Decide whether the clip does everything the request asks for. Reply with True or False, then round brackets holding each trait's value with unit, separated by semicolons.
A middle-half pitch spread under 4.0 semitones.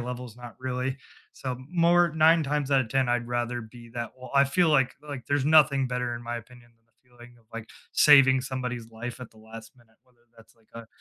True (2.4 semitones)